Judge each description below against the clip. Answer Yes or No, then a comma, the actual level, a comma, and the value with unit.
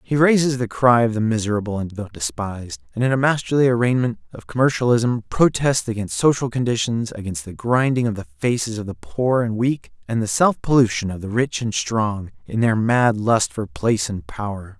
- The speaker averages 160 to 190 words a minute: No, average, 200 wpm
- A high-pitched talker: No, low, 115 Hz